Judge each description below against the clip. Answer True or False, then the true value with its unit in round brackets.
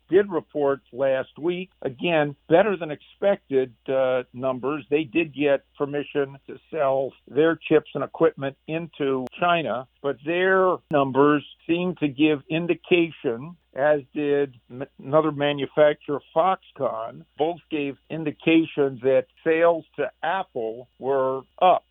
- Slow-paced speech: True (120 wpm)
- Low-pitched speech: False (145 Hz)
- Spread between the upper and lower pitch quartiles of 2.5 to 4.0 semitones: True (3.1 semitones)